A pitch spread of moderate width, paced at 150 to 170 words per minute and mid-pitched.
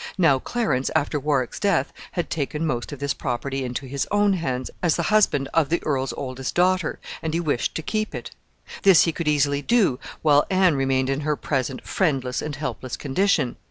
No: average, 4.3 semitones; average, 195 wpm; medium, 145 Hz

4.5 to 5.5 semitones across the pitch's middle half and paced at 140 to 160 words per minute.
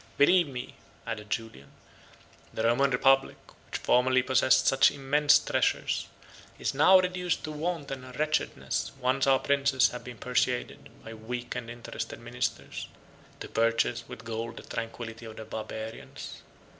No: average, 3.4 semitones; average, 145 wpm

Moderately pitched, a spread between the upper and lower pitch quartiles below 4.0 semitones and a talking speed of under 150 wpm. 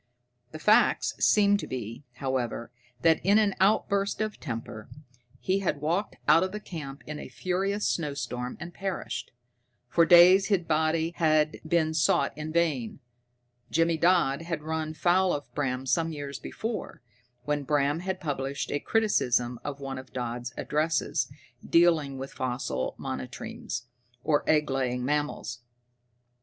No: medium, 155 Hz; average, 4.5 semitones; average, 140 wpm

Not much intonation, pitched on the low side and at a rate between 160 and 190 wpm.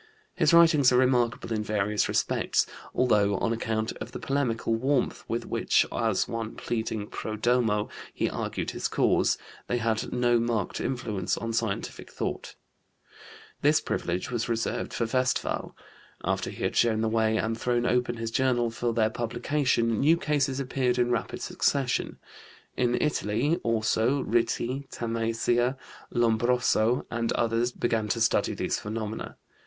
No: narrow, 1.9 semitones; low, 115 Hz; average, 145 wpm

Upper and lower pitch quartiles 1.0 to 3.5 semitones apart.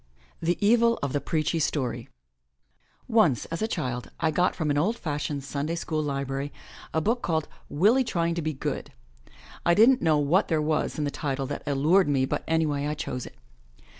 Yes: average, 3.2 semitones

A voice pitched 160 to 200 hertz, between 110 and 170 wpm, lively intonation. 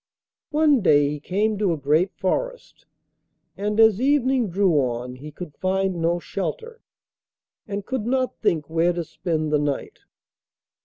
Yes: medium, 185 Hz; average, 150 wpm; wide, 6.3 semitones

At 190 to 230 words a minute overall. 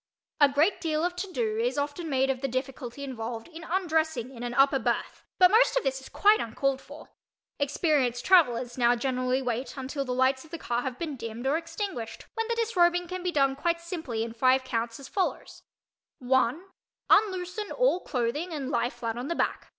Yes: average, 195 wpm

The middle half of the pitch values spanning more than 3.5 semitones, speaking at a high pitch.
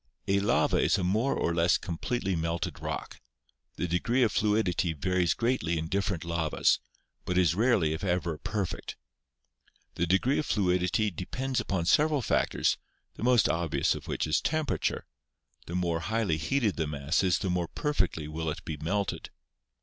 No: average, 4.6 semitones; very low, 90 Hz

